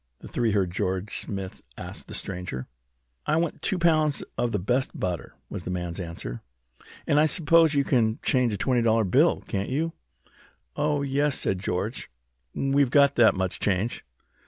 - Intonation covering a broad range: Yes, wide, 7.2 semitones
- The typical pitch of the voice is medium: No, low, 115 Hz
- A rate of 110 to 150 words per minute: No, average, 170 wpm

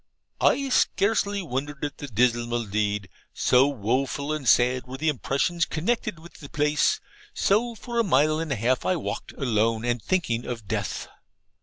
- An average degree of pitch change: No, wide, 5.8 semitones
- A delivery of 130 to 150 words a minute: No, average, 165 wpm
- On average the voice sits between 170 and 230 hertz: No, medium, 140 Hz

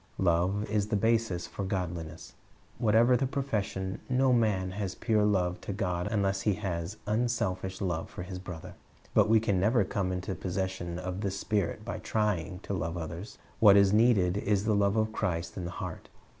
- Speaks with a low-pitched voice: Yes, low, 100 Hz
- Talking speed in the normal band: Yes, average, 185 wpm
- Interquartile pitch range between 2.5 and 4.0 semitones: Yes, average, 2.9 semitones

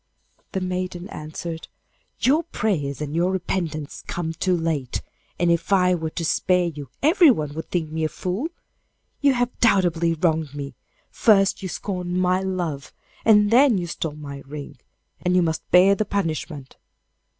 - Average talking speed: Yes, average, 160 wpm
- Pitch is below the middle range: No, medium, 175 Hz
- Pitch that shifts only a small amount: No, average, 3.4 semitones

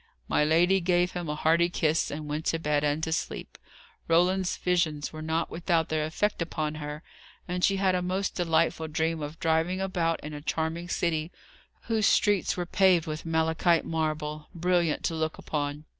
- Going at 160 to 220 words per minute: Yes, average, 180 wpm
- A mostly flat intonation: Yes, narrow, 2.3 semitones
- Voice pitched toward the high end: No, medium, 165 Hz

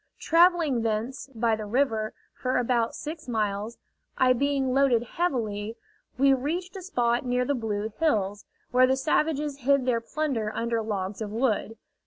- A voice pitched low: No, very high, 250 Hz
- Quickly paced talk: No, average, 155 wpm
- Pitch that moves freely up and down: No, average, 4.0 semitones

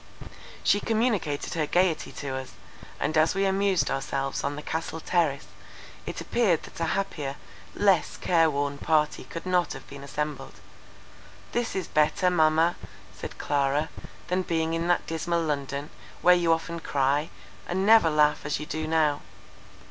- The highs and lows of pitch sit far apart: No, average, 3.4 semitones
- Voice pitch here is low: No, medium, 160 Hz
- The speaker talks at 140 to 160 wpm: Yes, average, 155 wpm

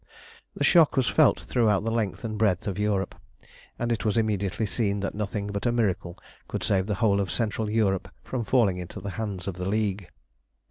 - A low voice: Yes, low, 105 Hz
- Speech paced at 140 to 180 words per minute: No, average, 200 wpm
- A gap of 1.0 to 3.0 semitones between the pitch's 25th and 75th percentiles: Yes, narrow, 2.6 semitones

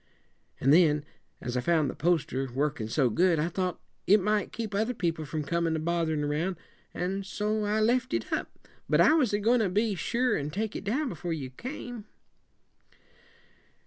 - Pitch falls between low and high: Yes, medium, 180 Hz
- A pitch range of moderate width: No, wide, 5.9 semitones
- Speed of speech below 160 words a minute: No, average, 185 wpm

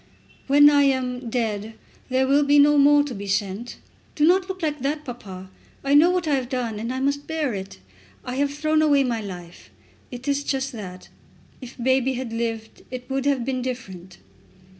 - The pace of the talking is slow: No, average, 195 wpm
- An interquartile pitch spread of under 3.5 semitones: No, average, 4.0 semitones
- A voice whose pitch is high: Yes, very high, 260 Hz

